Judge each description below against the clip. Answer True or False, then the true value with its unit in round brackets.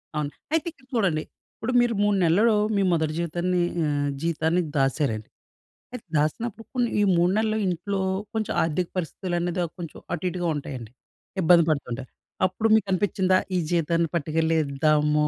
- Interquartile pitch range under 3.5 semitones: False (4.5 semitones)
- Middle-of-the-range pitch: True (170 Hz)